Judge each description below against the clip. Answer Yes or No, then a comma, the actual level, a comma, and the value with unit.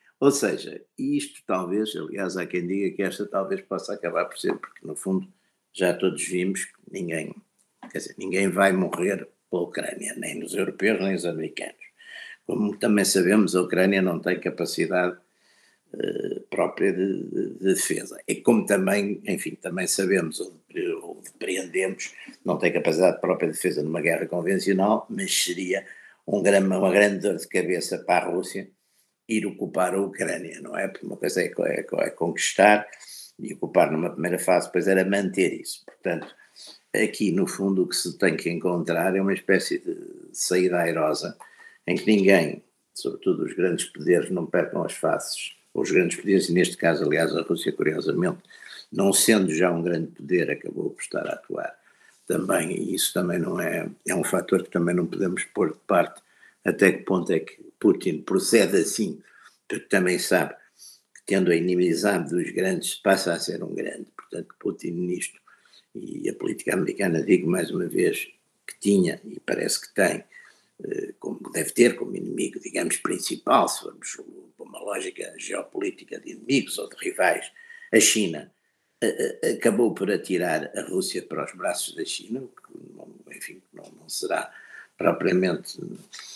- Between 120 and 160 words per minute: No, average, 170 wpm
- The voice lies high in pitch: Yes, very high, 330 Hz